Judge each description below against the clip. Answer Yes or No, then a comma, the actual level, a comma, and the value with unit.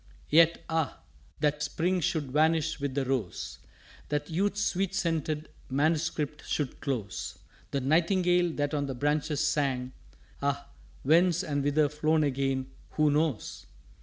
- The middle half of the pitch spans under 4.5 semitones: Yes, average, 2.7 semitones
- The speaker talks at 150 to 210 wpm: No, slow, 135 wpm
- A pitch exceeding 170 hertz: No, medium, 150 Hz